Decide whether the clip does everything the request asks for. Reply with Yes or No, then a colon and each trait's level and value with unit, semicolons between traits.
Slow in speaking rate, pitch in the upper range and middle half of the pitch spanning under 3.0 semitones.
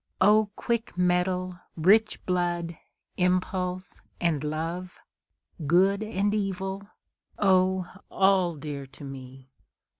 No: slow, 95 wpm; medium, 180 Hz; narrow, 2.4 semitones